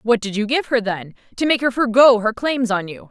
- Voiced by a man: No, female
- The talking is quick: Yes, fast, 270 wpm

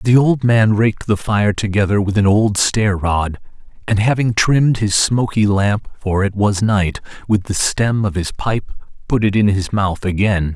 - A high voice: No, low, 105 Hz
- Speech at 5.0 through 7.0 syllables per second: No, 4.3 syllables/s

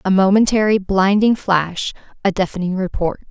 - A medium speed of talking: No, slow, 125 wpm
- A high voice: Yes, high, 195 Hz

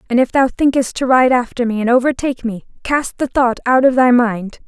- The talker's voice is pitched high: Yes, very high, 250 Hz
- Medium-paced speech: No, fast, 230 wpm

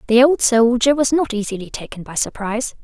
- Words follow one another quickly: No, average, 190 wpm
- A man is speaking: No, female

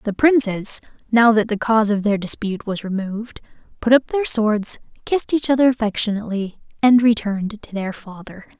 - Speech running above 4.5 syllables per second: Yes, 5.5 syllables/s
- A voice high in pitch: Yes, high, 220 Hz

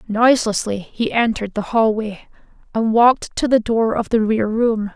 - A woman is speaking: Yes, female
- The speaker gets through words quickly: No, average, 170 wpm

